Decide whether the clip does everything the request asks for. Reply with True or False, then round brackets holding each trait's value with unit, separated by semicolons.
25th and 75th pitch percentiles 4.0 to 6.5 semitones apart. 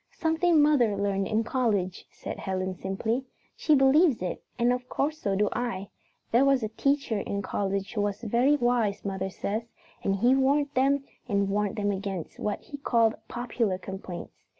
True (5.1 semitones)